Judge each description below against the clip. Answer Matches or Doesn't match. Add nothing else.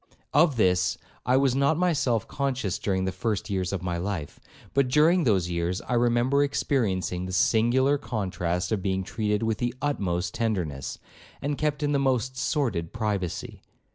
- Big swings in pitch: Matches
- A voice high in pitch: Doesn't match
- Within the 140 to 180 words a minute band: Matches